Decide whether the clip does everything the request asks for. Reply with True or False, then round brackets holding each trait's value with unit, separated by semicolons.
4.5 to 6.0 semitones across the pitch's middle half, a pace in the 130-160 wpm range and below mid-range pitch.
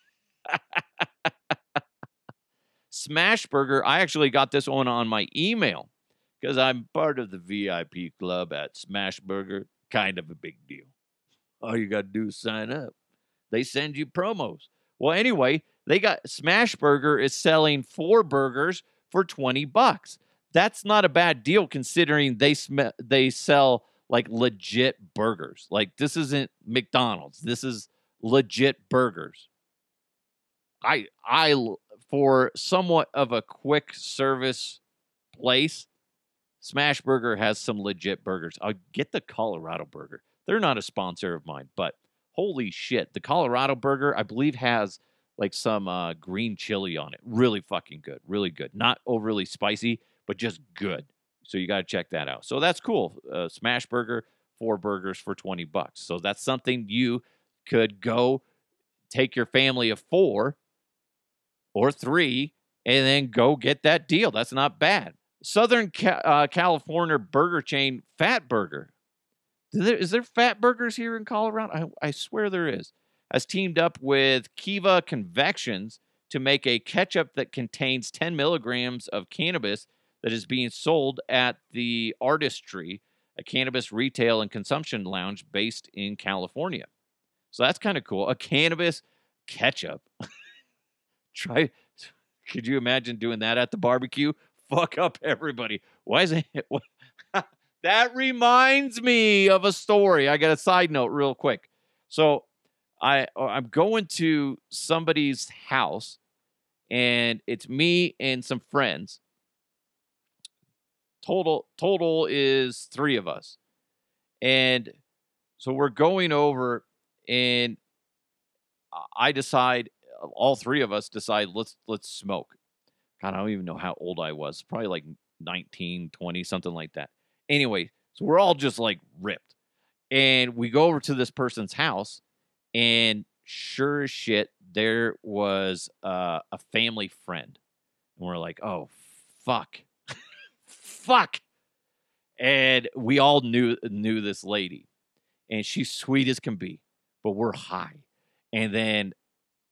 True (5.2 semitones; 140 wpm; 130 Hz)